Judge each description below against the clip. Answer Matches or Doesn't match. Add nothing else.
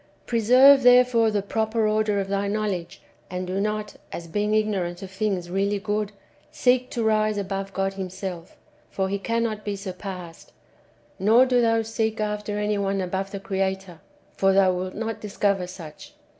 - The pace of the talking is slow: Doesn't match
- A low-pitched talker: Doesn't match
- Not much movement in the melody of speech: Matches